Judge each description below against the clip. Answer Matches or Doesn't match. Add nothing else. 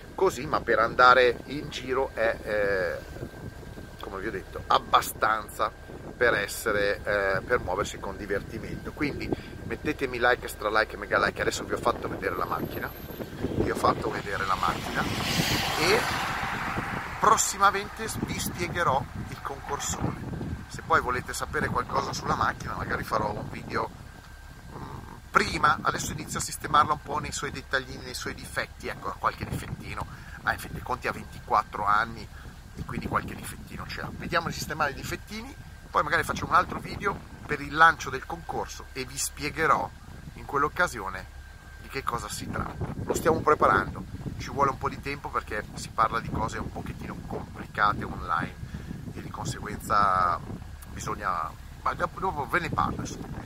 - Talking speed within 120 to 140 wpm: Doesn't match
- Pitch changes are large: Matches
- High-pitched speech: Doesn't match